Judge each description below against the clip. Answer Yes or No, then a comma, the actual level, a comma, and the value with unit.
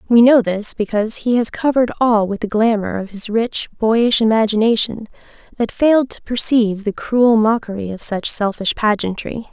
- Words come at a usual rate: Yes, average, 170 wpm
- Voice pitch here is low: No, high, 220 Hz